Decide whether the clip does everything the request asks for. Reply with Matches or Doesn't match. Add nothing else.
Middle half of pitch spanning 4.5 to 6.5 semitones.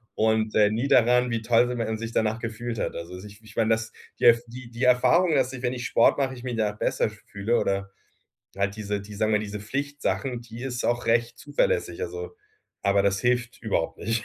Doesn't match